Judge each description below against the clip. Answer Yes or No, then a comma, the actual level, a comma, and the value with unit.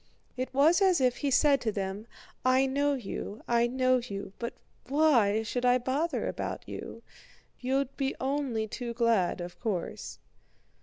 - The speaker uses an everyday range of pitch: Yes, average, 3.6 semitones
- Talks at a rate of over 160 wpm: No, average, 155 wpm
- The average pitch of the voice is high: Yes, very high, 250 Hz